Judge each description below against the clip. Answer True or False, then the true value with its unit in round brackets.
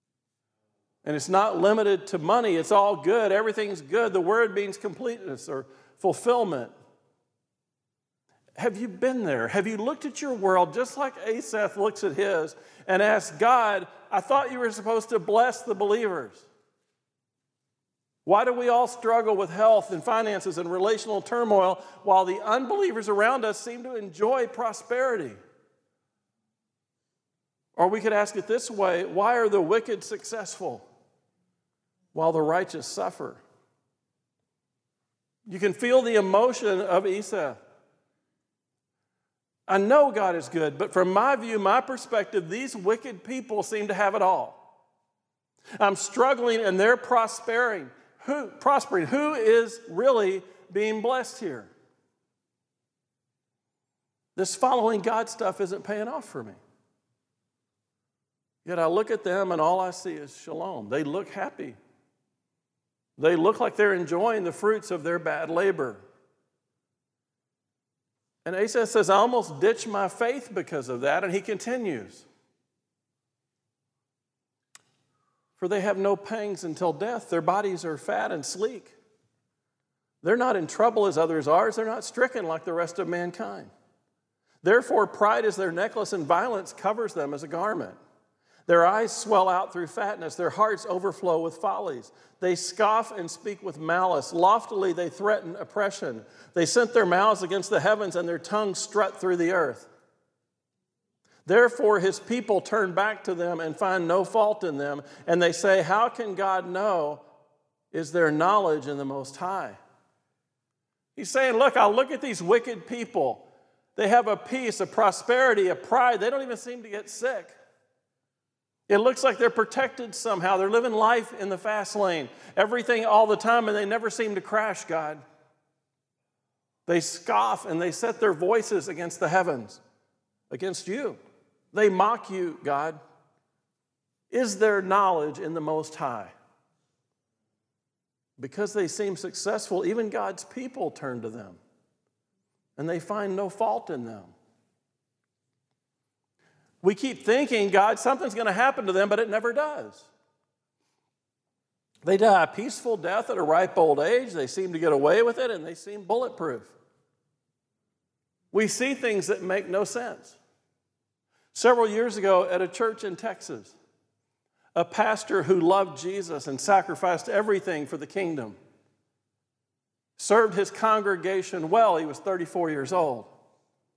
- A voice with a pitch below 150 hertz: False (205 Hz)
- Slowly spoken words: False (150 wpm)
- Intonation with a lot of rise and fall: False (4.8 semitones)